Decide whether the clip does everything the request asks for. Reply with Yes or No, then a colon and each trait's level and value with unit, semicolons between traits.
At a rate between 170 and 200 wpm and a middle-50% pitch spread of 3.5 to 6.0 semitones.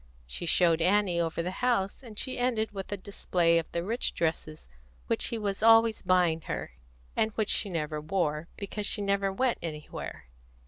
Yes: average, 180 wpm; average, 4.4 semitones